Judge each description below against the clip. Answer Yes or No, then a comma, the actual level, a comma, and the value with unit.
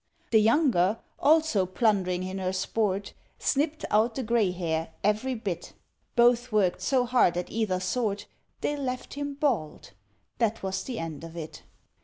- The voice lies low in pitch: No, high, 215 Hz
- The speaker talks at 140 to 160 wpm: Yes, average, 155 wpm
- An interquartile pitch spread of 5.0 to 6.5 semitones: Yes, average, 5.3 semitones